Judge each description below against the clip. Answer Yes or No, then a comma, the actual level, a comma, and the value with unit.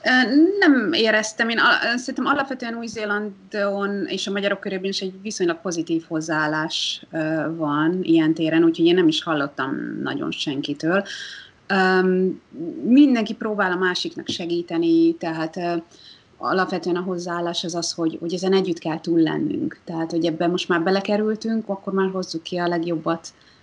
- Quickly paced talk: No, average, 140 wpm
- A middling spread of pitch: Yes, average, 4.5 semitones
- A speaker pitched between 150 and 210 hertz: Yes, medium, 185 Hz